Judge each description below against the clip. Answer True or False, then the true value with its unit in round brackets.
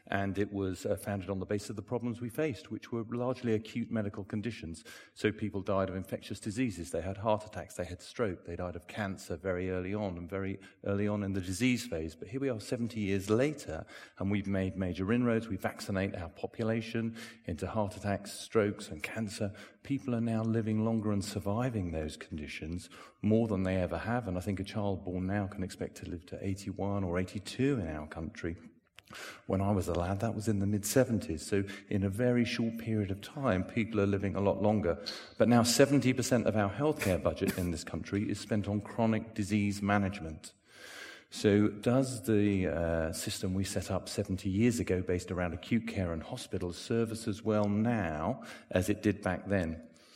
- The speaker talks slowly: False (200 wpm)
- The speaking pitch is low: True (100 Hz)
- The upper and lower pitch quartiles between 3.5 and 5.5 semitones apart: False (3.1 semitones)